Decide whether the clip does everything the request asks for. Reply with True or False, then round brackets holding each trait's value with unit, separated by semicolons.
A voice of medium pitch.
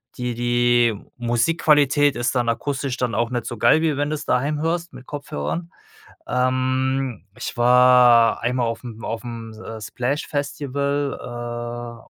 False (125 Hz)